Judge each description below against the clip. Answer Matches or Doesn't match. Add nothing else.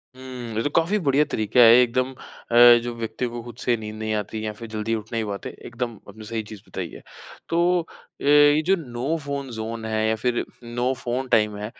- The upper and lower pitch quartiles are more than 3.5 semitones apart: Doesn't match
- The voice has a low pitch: Matches